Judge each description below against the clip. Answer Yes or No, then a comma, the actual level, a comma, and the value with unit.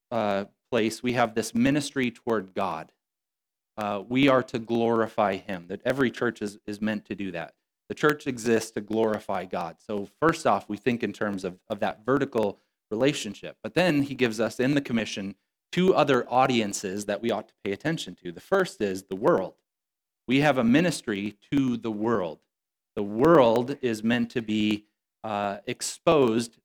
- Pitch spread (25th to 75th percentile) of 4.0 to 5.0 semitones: No, average, 3.3 semitones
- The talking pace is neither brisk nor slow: Yes, average, 180 wpm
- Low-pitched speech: Yes, low, 115 Hz